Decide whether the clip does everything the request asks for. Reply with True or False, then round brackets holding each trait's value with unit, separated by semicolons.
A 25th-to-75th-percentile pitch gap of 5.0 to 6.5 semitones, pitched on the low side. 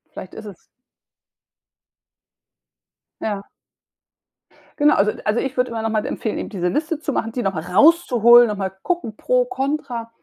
False (5.4 semitones; 230 Hz)